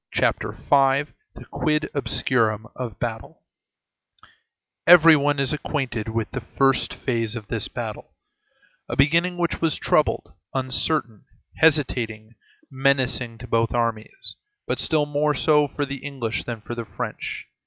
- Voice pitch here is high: No, low, 135 Hz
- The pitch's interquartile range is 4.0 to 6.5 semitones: Yes, average, 4.3 semitones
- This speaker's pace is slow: Yes, slow, 130 wpm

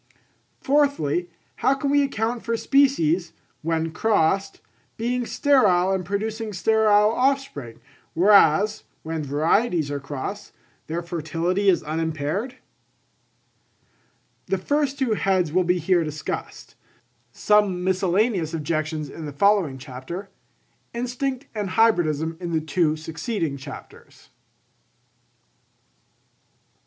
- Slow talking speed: Yes, slow, 105 wpm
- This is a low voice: No, medium, 185 Hz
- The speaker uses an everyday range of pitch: No, wide, 5.7 semitones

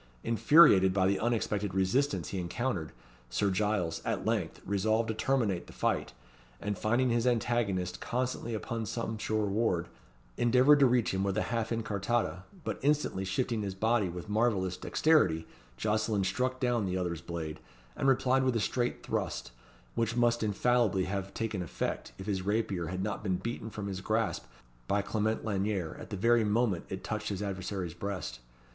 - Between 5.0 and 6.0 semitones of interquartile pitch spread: No, average, 3.8 semitones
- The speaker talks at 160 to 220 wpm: Yes, average, 170 wpm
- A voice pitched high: No, low, 105 Hz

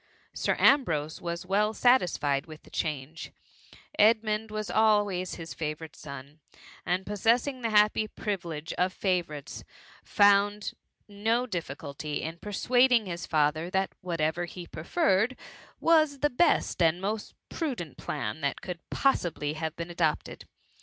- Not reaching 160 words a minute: Yes, average, 140 wpm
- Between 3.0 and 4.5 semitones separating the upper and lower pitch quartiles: No, average, 5.2 semitones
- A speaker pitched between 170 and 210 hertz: Yes, medium, 185 Hz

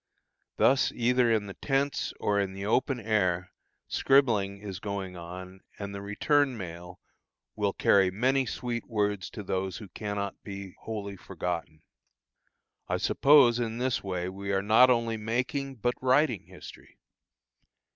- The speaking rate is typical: Yes, average, 145 wpm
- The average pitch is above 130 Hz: No, low, 105 Hz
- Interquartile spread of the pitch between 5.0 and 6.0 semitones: No, average, 4.2 semitones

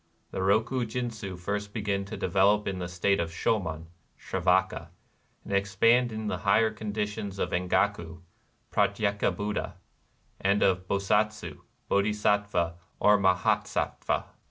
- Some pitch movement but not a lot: No, narrow, 2.1 semitones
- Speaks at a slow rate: Yes, slow, 130 wpm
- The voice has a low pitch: Yes, low, 100 Hz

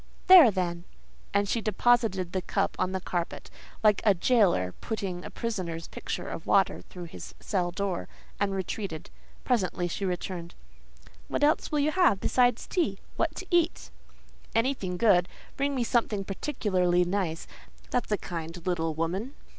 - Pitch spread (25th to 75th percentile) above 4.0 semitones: Yes, average, 5.0 semitones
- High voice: Yes, high, 195 Hz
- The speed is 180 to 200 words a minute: No, average, 145 wpm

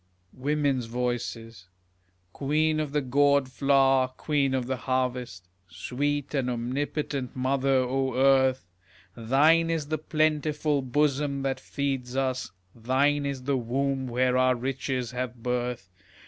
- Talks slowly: Yes, slow, 125 wpm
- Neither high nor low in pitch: No, low, 130 Hz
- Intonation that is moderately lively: No, narrow, 2.2 semitones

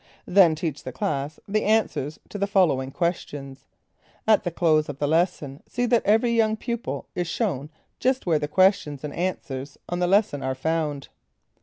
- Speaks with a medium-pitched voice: Yes, medium, 165 Hz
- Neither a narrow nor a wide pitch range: No, wide, 5.8 semitones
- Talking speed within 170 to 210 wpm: Yes, average, 175 wpm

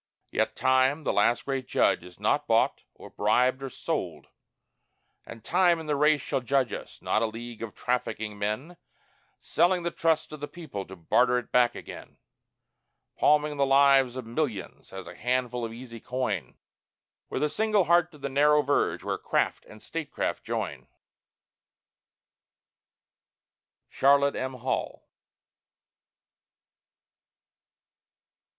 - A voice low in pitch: Yes, low, 130 Hz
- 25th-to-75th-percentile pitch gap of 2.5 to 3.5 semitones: No, average, 4.1 semitones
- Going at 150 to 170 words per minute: No, slow, 135 wpm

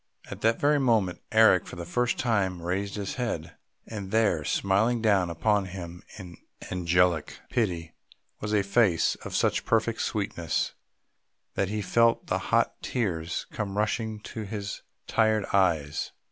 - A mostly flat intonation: No, average, 3.8 semitones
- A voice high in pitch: No, low, 100 Hz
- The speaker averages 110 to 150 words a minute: Yes, average, 145 wpm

